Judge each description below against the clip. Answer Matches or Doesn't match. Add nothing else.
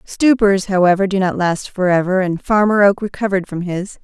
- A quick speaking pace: Doesn't match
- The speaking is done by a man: Doesn't match